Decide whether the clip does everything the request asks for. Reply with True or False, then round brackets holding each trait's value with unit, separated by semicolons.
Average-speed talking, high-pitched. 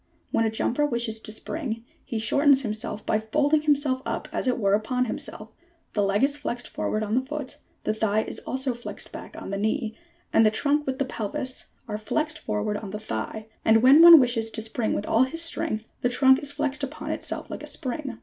False (215 wpm; 240 Hz)